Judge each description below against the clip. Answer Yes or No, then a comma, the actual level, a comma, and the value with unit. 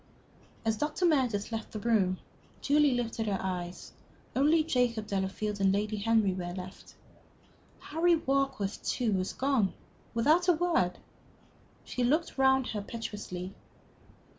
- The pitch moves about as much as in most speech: No, wide, 5.7 semitones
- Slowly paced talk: Yes, slow, 130 wpm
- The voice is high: Yes, high, 225 Hz